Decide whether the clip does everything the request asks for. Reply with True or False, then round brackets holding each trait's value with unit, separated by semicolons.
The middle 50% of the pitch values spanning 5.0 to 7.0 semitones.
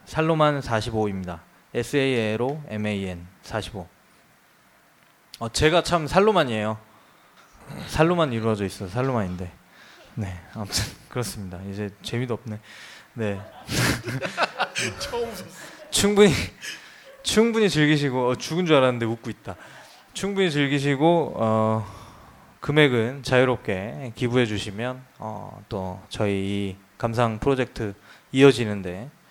True (5.5 semitones)